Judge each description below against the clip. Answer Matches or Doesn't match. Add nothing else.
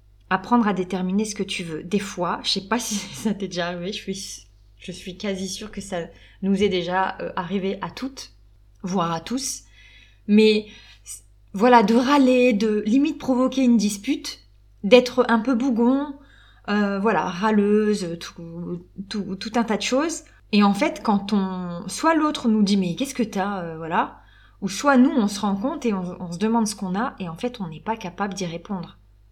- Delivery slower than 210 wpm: Matches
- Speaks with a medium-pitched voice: Doesn't match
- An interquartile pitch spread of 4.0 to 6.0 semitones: Matches